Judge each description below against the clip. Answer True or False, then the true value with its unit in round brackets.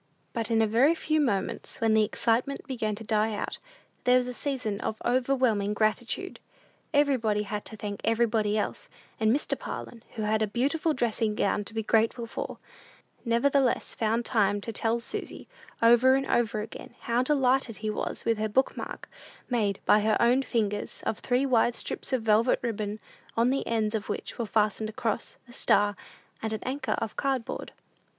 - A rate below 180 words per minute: False (185 wpm)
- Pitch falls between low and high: False (225 Hz)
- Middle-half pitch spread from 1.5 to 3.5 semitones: True (2.8 semitones)